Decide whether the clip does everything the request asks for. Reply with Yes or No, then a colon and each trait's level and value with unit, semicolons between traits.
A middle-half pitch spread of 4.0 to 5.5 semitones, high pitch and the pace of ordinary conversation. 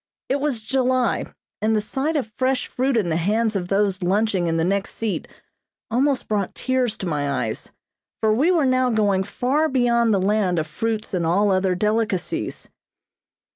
Yes: average, 5.1 semitones; high, 215 Hz; average, 175 wpm